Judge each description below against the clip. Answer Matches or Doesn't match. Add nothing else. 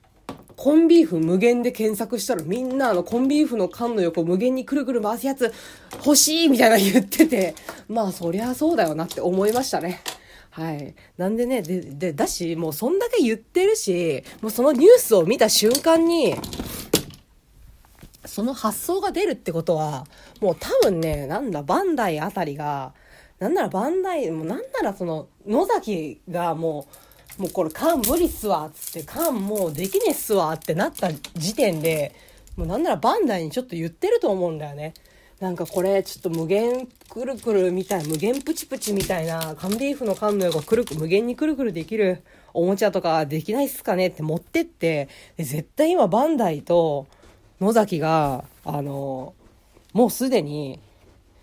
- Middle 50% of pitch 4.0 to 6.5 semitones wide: Doesn't match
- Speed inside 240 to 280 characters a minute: Doesn't match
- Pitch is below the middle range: Doesn't match